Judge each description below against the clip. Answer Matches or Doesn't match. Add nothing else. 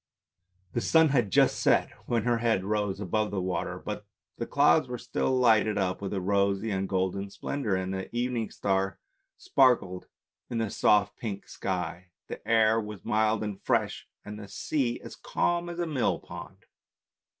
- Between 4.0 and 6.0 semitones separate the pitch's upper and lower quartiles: Doesn't match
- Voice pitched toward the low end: Matches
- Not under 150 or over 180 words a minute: Matches